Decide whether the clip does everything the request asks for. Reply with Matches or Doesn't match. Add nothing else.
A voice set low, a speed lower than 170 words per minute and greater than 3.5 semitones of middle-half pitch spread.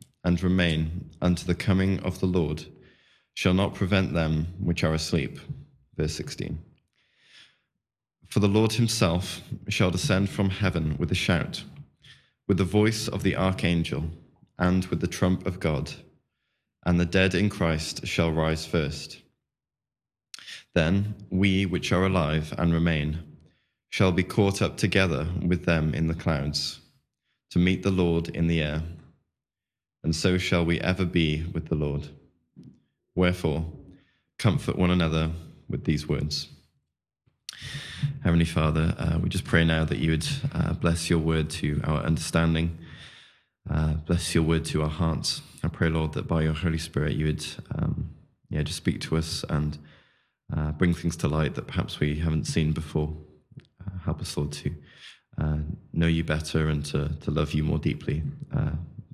Doesn't match